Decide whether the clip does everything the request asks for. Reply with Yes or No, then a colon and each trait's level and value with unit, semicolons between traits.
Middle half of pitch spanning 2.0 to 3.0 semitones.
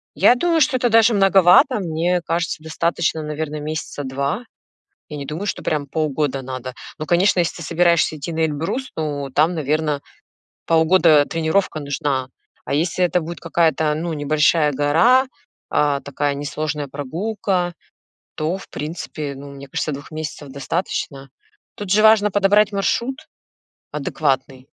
No: average, 3.7 semitones